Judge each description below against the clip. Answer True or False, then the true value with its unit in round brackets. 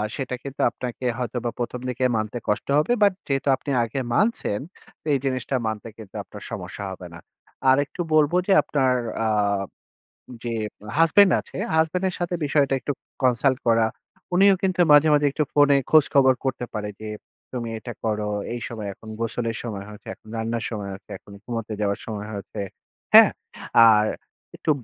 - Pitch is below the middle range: True (125 Hz)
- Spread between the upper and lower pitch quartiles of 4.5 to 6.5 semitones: True (4.8 semitones)